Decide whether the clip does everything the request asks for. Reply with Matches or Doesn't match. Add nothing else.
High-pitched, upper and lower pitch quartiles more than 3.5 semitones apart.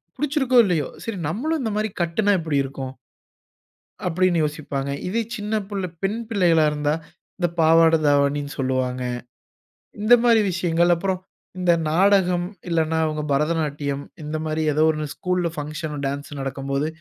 Doesn't match